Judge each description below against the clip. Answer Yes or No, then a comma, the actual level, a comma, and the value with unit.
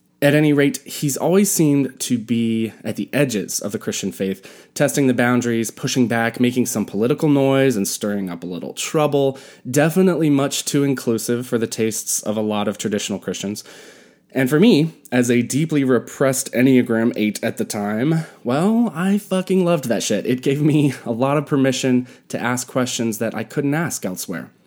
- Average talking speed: Yes, average, 185 wpm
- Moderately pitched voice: No, low, 130 Hz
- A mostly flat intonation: No, average, 4.4 semitones